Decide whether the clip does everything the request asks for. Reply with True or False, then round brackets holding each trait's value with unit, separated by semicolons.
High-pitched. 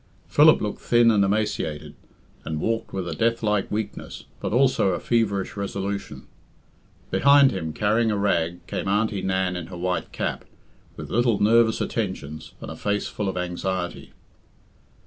False (100 Hz)